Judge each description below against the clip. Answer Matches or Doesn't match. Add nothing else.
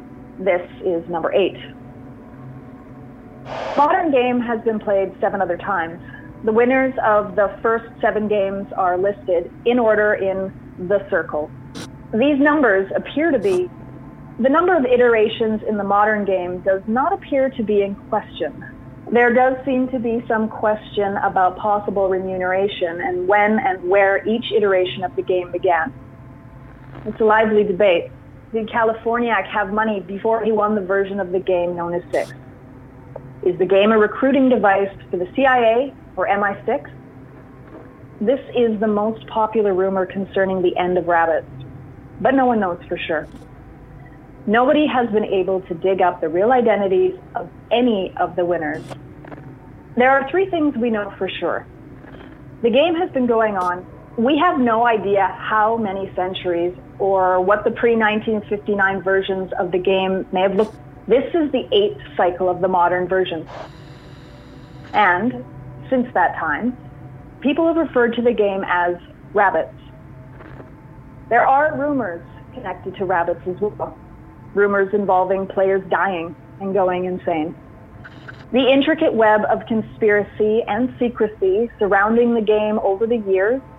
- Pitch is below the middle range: Doesn't match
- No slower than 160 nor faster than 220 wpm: Doesn't match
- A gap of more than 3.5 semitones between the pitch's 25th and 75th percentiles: Matches